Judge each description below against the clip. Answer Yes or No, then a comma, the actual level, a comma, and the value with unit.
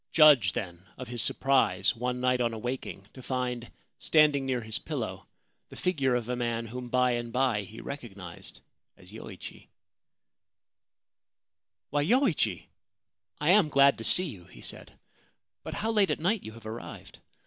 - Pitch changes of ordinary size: Yes, average, 3.6 semitones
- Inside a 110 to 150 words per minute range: No, average, 165 wpm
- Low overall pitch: Yes, low, 125 Hz